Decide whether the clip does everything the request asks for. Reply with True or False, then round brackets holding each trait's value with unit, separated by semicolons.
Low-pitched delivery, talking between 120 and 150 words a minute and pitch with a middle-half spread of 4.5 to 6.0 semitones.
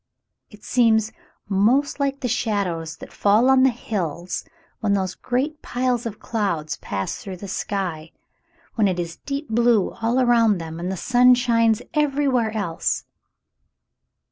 False (220 Hz; 145 wpm; 4.8 semitones)